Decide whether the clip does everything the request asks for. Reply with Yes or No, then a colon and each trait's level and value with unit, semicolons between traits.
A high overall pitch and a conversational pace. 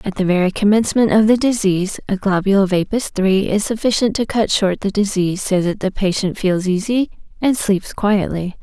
Yes: high, 200 Hz; average, 195 wpm